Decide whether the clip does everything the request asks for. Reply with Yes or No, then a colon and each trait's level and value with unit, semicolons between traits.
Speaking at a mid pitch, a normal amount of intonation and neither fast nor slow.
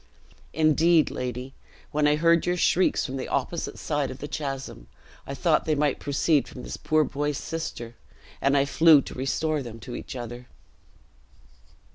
Yes: medium, 145 Hz; average, 3.1 semitones; average, 165 wpm